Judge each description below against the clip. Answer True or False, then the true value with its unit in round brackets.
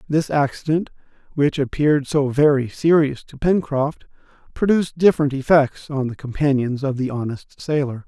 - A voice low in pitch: False (145 Hz)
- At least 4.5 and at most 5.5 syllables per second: True (5.0 syllables/s)